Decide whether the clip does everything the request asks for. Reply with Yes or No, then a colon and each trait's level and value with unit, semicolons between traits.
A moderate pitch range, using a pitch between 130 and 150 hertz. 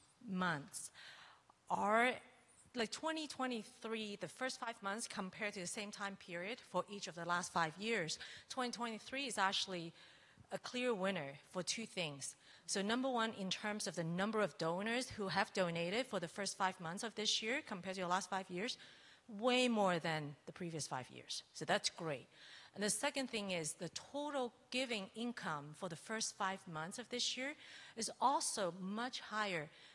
No: average, 4.7 semitones; high, 200 Hz